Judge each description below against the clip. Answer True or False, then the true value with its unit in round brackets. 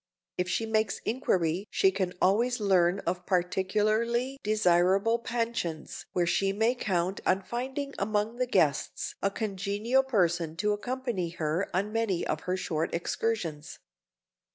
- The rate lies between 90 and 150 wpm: True (135 wpm)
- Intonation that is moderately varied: True (4.2 semitones)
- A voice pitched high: True (200 Hz)